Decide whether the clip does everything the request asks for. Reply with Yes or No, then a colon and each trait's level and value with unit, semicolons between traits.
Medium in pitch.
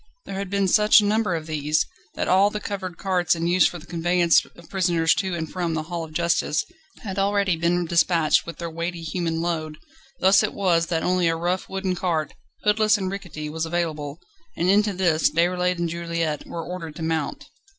Yes: medium, 175 Hz